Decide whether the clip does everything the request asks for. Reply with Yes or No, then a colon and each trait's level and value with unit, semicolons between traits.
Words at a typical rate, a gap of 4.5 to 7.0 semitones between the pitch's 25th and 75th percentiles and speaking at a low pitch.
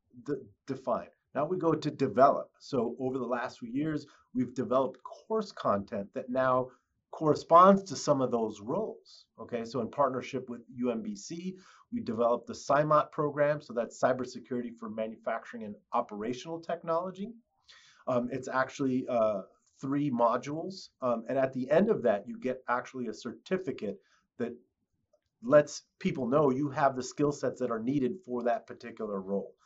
Yes: average, 160 wpm; average, 5.2 semitones; low, 130 Hz